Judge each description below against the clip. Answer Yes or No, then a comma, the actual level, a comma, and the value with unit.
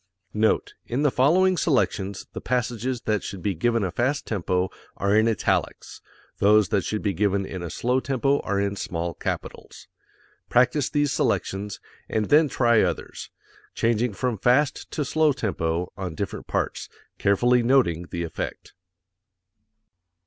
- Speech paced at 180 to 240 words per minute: No, average, 150 wpm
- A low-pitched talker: Yes, low, 110 Hz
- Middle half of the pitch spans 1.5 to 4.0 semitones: No, average, 4.8 semitones